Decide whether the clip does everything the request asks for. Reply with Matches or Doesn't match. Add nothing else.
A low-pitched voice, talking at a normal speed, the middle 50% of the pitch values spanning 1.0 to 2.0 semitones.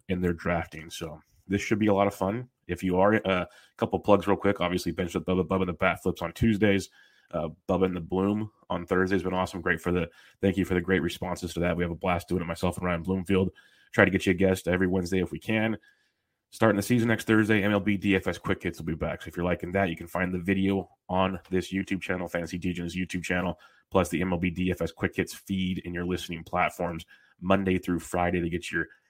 Doesn't match